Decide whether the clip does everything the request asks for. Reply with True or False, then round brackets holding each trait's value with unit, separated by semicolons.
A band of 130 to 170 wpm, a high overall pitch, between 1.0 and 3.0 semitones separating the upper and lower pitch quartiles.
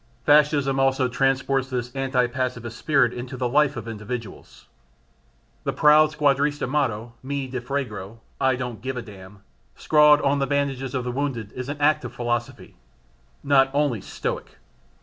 False (155 wpm; 130 Hz; 2.7 semitones)